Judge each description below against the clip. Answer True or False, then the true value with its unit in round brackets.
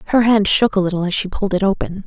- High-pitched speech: True (200 Hz)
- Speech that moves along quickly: True (290 wpm)